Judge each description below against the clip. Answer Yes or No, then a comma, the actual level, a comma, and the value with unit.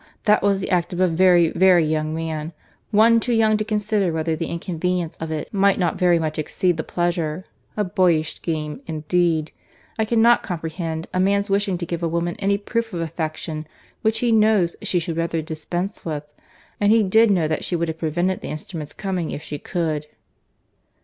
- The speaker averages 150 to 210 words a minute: Yes, average, 190 wpm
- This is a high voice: No, medium, 175 Hz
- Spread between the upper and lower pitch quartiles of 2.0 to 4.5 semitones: Yes, average, 3.7 semitones